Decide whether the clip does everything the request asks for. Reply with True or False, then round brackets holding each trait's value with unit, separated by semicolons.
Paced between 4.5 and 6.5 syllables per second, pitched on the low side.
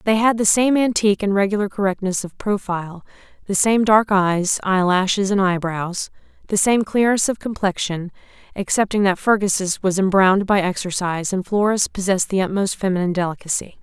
False (5.5 syllables/s; 195 Hz)